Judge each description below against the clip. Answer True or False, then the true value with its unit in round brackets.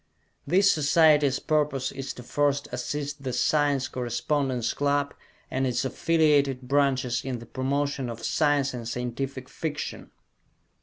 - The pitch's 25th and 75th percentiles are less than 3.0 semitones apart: True (2.4 semitones)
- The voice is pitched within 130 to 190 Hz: True (140 Hz)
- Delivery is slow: True (125 wpm)